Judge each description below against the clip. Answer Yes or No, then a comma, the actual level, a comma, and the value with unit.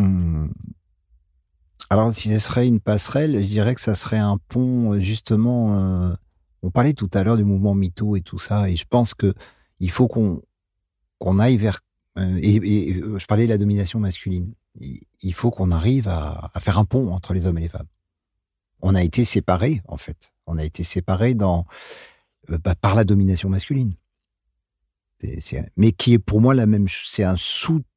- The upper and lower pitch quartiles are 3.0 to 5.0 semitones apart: Yes, average, 3.4 semitones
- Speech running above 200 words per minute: No, average, 195 wpm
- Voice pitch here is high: No, low, 100 Hz